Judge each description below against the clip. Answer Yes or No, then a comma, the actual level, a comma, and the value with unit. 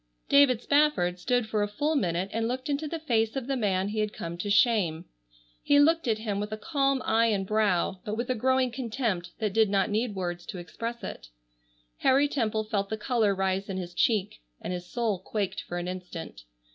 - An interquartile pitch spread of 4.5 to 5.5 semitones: Yes, average, 4.8 semitones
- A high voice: Yes, high, 215 Hz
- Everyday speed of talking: No, fast, 210 wpm